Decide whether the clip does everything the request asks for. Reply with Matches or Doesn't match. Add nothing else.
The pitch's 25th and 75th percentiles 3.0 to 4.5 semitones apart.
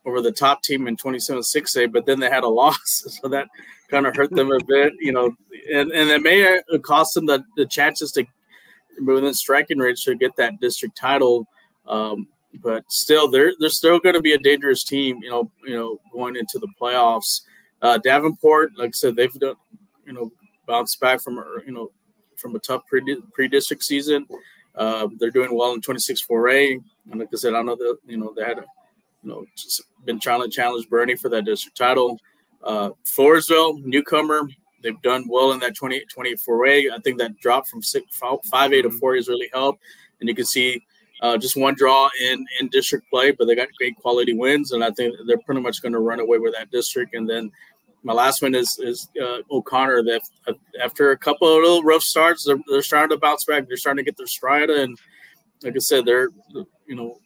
Matches